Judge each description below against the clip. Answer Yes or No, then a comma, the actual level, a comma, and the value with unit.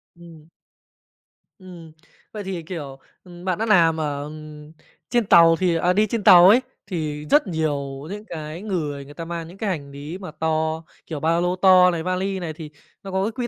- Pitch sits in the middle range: Yes, medium, 170 Hz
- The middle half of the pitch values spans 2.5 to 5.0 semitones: Yes, average, 3.2 semitones